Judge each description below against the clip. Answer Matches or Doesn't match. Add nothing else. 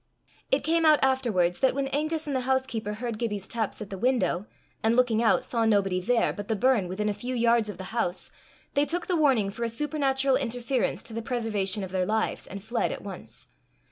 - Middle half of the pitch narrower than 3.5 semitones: Doesn't match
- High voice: Matches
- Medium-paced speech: Doesn't match